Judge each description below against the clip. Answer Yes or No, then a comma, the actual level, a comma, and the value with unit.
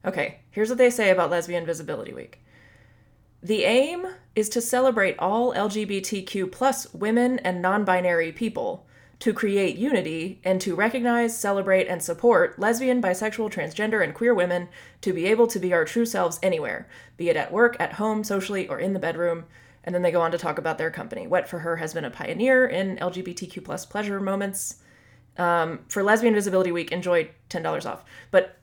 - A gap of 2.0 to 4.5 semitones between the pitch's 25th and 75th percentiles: Yes, average, 4.2 semitones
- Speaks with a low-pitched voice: No, high, 190 Hz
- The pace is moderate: Yes, average, 185 wpm